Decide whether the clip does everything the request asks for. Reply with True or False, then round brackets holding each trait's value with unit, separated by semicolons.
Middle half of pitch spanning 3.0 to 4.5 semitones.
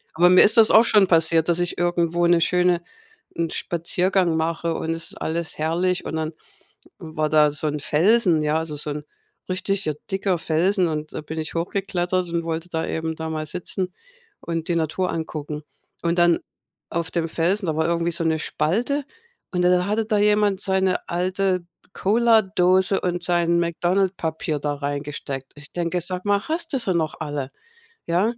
False (2.6 semitones)